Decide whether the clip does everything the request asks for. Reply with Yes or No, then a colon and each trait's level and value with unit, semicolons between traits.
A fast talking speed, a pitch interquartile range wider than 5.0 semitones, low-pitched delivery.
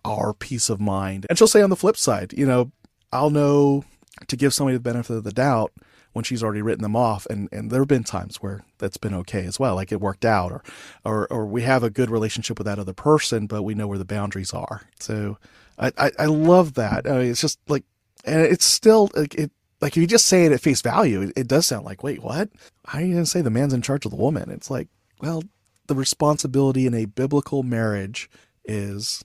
Yes: fast, 240 wpm; wide, 5.4 semitones; low, 125 Hz